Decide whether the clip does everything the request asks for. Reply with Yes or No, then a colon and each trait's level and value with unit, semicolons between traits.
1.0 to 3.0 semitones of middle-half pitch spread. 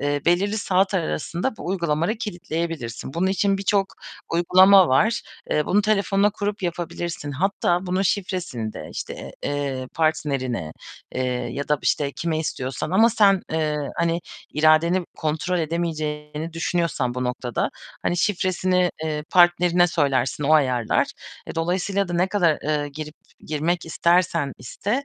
No: average, 3.7 semitones